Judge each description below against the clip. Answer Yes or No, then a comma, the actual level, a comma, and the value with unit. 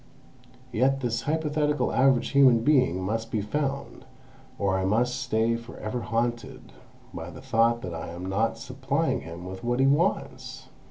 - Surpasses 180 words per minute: No, average, 160 wpm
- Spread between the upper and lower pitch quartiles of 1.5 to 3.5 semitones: No, average, 3.9 semitones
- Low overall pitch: Yes, low, 120 Hz